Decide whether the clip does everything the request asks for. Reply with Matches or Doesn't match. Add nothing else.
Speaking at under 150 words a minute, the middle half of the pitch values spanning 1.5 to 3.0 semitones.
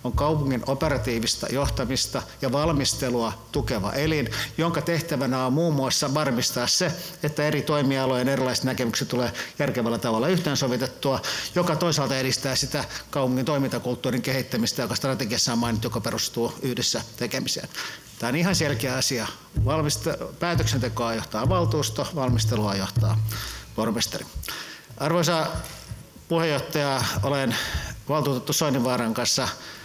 Doesn't match